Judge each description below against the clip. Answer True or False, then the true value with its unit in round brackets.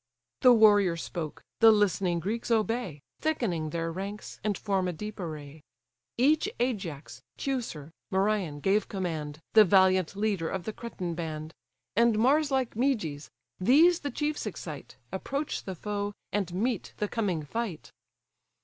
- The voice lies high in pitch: True (200 Hz)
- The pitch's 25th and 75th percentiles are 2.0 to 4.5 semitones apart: False (5.5 semitones)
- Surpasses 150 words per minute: False (140 wpm)